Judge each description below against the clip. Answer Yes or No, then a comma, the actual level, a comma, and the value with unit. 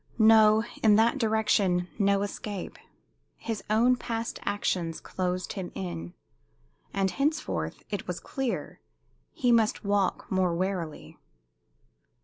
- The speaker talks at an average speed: No, slow, 115 wpm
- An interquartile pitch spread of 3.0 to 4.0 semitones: Yes, average, 3.7 semitones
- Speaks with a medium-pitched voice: No, high, 205 Hz